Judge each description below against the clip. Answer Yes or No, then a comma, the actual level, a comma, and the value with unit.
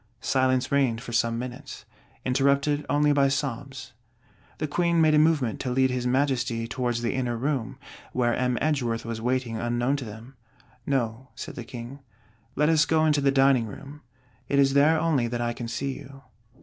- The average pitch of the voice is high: No, low, 130 Hz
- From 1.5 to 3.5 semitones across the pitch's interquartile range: Yes, average, 2.9 semitones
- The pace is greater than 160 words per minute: Yes, average, 180 wpm